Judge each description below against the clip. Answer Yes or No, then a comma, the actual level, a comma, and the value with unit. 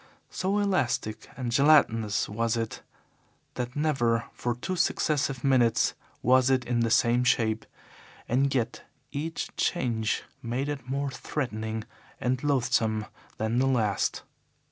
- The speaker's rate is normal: No, slow, 120 wpm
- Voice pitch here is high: No, low, 125 Hz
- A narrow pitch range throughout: No, average, 3.4 semitones